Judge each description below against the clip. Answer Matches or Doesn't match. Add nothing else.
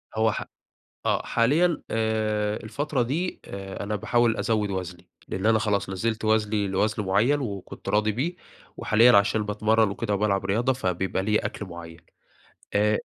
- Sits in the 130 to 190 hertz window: Doesn't match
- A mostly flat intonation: Matches